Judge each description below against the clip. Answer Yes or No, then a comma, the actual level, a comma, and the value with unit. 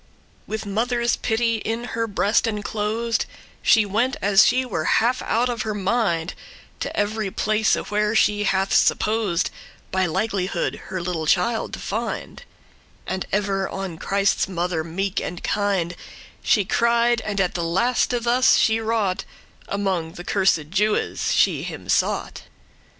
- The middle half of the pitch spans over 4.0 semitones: No, average, 3.2 semitones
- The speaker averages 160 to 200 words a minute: No, average, 145 wpm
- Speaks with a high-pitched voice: Yes, high, 205 Hz